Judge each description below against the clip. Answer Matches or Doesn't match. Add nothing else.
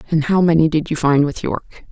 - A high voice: Doesn't match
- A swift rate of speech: Matches